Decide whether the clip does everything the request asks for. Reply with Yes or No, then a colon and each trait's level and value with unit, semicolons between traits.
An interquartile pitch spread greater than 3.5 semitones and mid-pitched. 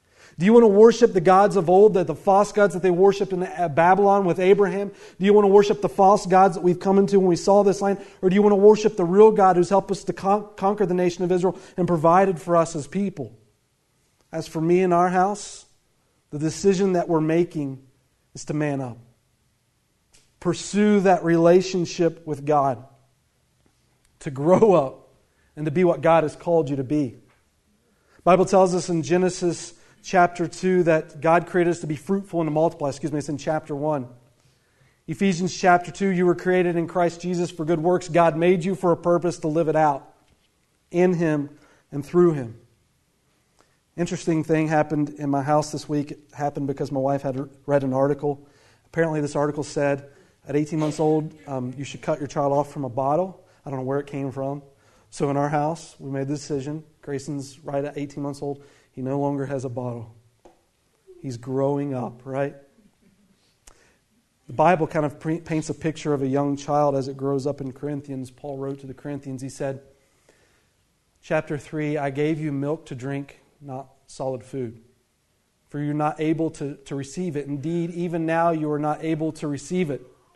Yes: average, 4.2 semitones; medium, 155 Hz